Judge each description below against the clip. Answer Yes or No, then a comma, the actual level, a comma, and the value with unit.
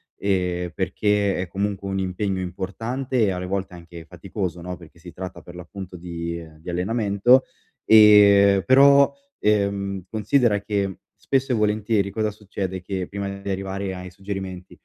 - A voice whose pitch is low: Yes, low, 100 Hz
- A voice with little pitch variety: Yes, narrow, 2.3 semitones